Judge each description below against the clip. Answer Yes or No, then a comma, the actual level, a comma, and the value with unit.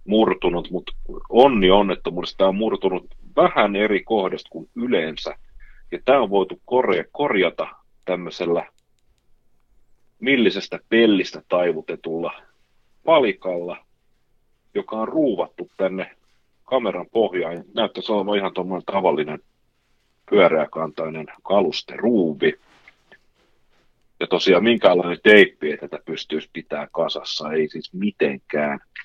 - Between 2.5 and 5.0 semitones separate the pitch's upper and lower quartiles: No, wide, 5.6 semitones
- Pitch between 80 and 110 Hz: Yes, very low, 95 Hz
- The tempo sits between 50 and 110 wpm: Yes, average, 100 wpm